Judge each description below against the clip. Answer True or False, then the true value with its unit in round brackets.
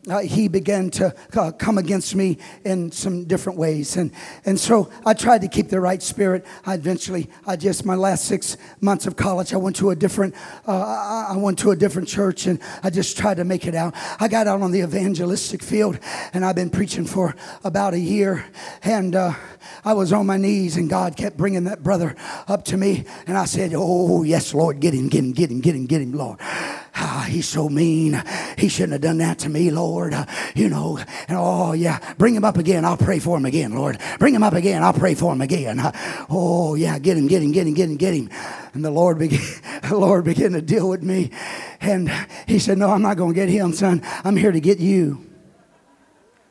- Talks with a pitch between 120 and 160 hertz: False (185 Hz)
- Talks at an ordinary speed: False (225 wpm)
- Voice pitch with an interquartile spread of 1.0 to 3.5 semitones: True (2.5 semitones)